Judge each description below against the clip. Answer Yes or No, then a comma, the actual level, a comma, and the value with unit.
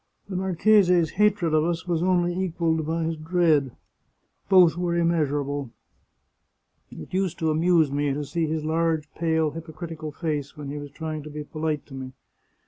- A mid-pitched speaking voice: Yes, medium, 160 Hz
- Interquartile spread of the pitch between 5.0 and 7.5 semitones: No, narrow, 2.4 semitones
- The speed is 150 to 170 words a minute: Yes, average, 165 wpm